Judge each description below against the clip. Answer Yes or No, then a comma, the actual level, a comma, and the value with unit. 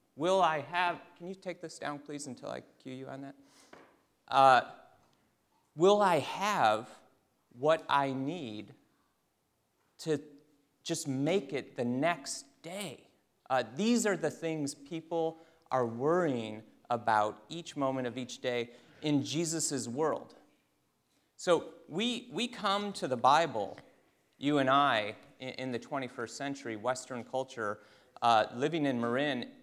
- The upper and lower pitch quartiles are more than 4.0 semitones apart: Yes, average, 4.6 semitones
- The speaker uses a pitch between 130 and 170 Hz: Yes, medium, 140 Hz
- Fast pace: No, slow, 135 wpm